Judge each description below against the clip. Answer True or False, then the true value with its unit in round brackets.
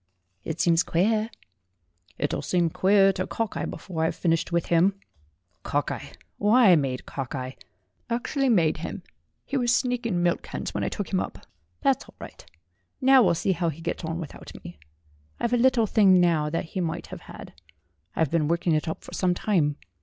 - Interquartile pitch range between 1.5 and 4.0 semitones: False (4.7 semitones)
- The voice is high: False (175 Hz)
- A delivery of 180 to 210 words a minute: True (185 wpm)